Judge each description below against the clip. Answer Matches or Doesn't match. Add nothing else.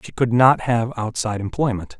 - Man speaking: Matches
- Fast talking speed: Doesn't match